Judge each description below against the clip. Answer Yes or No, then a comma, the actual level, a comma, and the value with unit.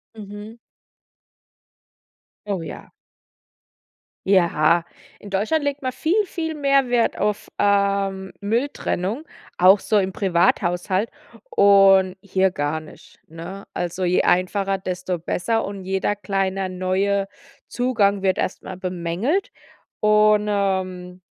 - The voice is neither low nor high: No, high, 195 Hz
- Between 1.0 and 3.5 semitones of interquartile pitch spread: Yes, narrow, 2.4 semitones